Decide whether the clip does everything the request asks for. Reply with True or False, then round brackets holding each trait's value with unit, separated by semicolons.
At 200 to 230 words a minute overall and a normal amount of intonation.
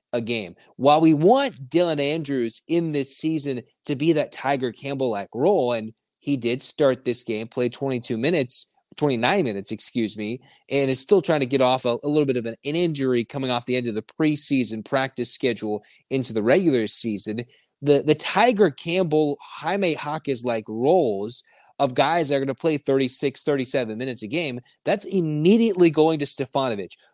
False (185 wpm; 4.1 semitones)